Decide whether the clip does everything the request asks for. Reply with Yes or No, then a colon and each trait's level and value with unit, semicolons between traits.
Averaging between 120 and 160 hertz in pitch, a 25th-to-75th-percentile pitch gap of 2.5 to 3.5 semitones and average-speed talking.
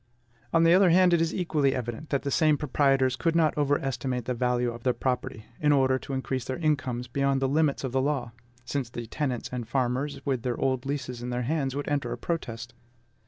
No: low, 135 Hz; average, 3.0 semitones; fast, 215 wpm